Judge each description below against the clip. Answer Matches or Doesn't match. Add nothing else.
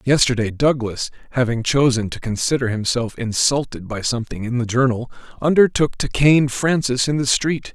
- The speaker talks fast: Doesn't match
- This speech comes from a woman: Doesn't match